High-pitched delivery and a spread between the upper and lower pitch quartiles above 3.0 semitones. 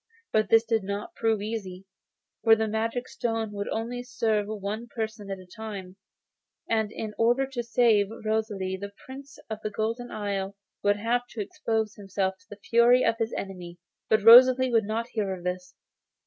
No: high, 220 Hz; narrow, 2.4 semitones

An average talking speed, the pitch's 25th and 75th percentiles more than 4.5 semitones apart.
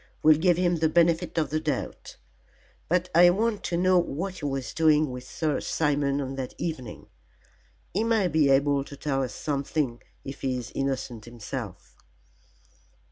No: average, 165 wpm; average, 4.1 semitones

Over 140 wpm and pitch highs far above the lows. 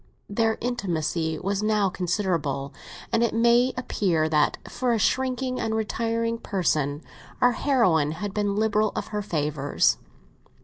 No: slow, 135 wpm; wide, 6.1 semitones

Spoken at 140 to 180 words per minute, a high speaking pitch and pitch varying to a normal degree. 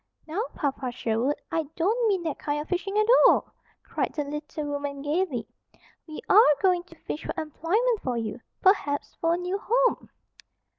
Yes: average, 175 wpm; very high, 320 Hz; average, 5.0 semitones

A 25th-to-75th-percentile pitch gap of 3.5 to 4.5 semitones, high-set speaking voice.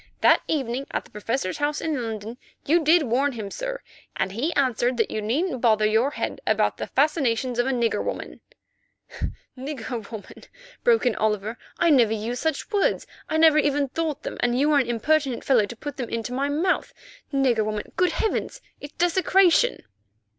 No: average, 5.0 semitones; very high, 265 Hz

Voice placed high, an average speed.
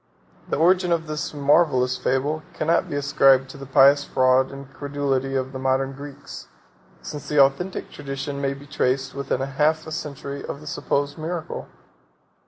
No: medium, 140 Hz; average, 165 wpm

